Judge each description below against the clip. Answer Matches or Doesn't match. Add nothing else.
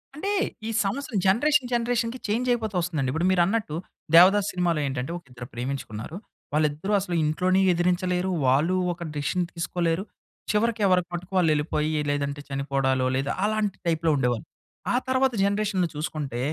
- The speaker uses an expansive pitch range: Matches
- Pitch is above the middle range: Doesn't match